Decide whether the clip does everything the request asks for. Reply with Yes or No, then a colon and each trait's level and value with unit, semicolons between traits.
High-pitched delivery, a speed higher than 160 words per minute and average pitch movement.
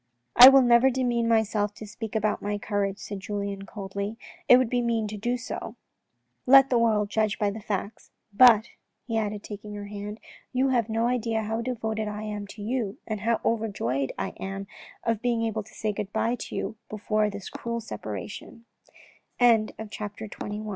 No: high, 215 Hz; average, 180 wpm; narrow, 2.2 semitones